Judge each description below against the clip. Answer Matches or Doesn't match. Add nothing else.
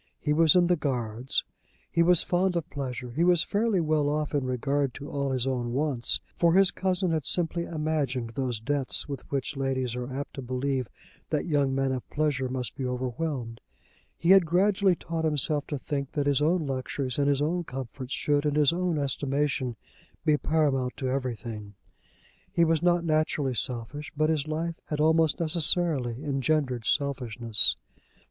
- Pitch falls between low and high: Matches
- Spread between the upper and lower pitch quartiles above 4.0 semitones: Doesn't match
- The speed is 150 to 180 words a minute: Matches